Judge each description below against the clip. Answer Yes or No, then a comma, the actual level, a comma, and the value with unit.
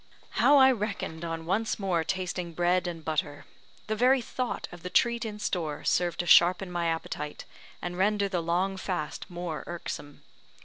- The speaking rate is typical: Yes, average, 170 wpm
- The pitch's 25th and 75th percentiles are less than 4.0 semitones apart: Yes, average, 3.3 semitones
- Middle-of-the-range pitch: Yes, medium, 180 Hz